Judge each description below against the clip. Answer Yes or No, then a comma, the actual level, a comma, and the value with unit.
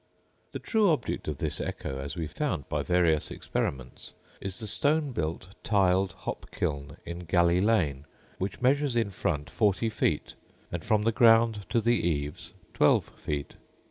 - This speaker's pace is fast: No, average, 155 wpm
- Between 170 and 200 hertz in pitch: No, very low, 95 Hz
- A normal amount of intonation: No, wide, 6.7 semitones